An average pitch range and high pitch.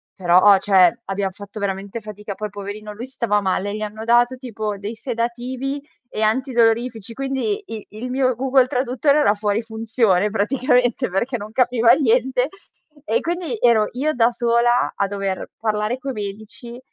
Yes: average, 3.3 semitones; high, 230 Hz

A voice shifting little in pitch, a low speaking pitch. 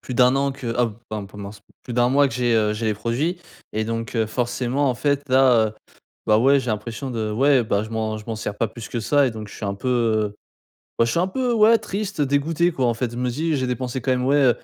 No: average, 3.8 semitones; low, 120 Hz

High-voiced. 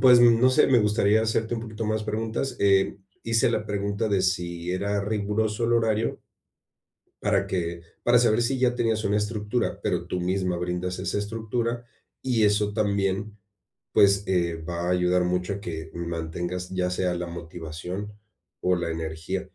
No: low, 100 Hz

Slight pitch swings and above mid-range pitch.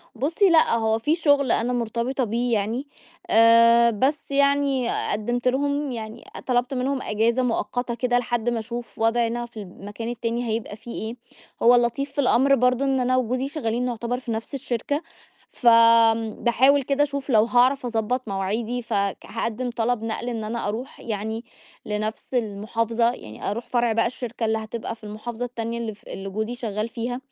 Yes: narrow, 2.1 semitones; high, 235 Hz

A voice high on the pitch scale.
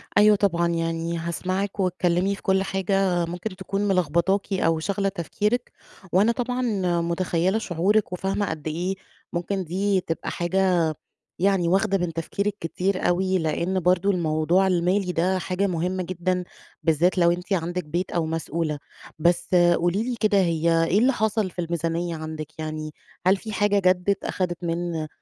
No: medium, 180 Hz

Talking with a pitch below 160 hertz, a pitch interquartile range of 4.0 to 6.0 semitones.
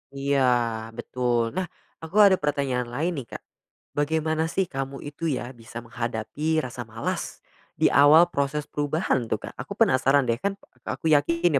Yes: medium, 140 Hz; average, 4.4 semitones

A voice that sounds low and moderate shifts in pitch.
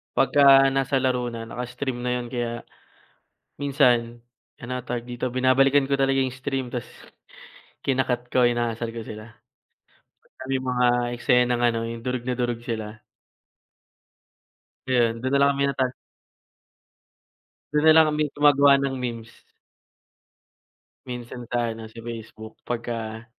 No: low, 125 Hz; narrow, 2.2 semitones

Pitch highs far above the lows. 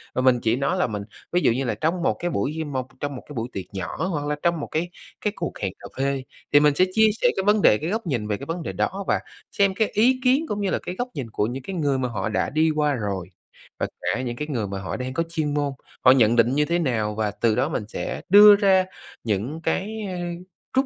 Yes: wide, 7.3 semitones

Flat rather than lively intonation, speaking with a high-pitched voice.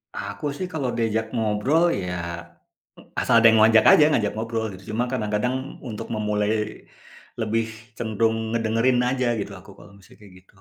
No: narrow, 2.0 semitones; low, 110 Hz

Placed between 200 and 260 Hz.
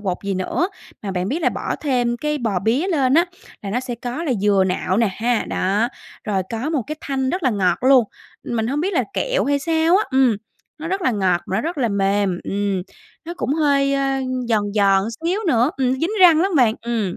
Yes: high, 245 Hz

